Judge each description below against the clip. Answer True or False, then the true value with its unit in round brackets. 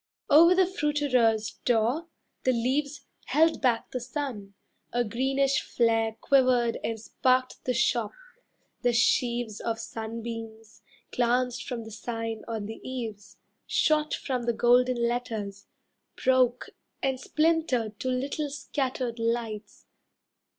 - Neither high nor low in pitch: False (245 Hz)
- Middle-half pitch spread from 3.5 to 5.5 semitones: False (2.7 semitones)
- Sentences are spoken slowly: True (120 wpm)